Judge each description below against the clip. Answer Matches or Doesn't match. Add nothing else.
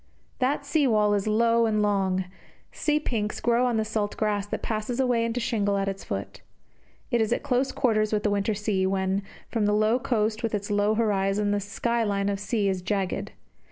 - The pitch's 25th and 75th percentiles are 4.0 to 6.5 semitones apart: Doesn't match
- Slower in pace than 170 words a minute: Doesn't match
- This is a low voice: Doesn't match